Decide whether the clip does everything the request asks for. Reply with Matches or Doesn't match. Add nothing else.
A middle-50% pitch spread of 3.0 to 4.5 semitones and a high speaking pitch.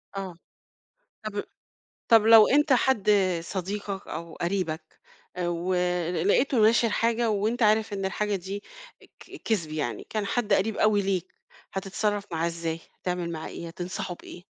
Matches